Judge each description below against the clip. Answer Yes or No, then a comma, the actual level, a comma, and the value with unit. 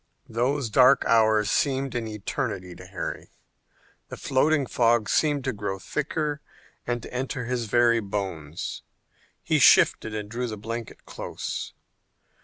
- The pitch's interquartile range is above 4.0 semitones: No, average, 3.7 semitones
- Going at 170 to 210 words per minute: No, slow, 135 wpm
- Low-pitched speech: Yes, low, 115 Hz